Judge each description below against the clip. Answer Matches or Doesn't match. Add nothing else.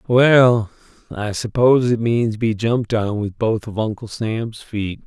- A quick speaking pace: Doesn't match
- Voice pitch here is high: Doesn't match